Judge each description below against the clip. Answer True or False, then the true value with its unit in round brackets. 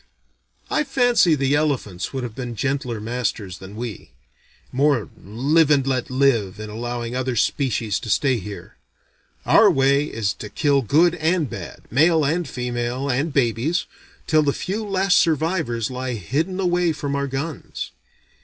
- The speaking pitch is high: False (135 Hz)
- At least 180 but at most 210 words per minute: False (155 wpm)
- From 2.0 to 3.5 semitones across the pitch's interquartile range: False (4.8 semitones)